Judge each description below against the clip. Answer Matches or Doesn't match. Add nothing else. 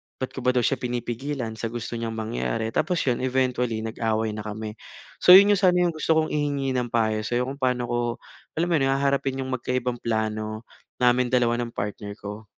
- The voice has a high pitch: Doesn't match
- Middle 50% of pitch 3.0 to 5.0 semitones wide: Matches